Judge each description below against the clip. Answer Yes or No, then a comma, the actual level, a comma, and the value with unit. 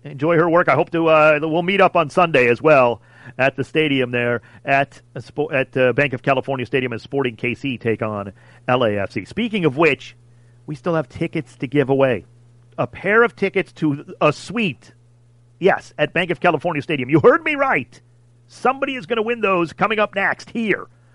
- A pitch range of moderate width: No, wide, 6.2 semitones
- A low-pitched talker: No, medium, 145 Hz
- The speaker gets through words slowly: No, average, 200 wpm